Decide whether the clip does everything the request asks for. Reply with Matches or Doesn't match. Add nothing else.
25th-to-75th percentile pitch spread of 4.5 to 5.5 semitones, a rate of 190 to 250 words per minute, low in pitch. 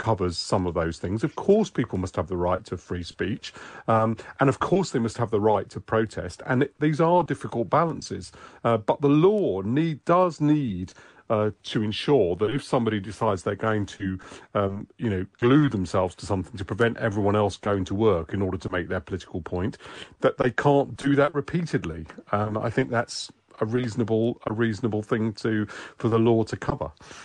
Matches